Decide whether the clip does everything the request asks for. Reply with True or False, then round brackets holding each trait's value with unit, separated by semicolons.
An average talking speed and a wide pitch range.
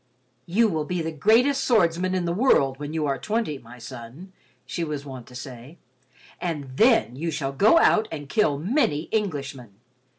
True (175 wpm; 6.8 semitones)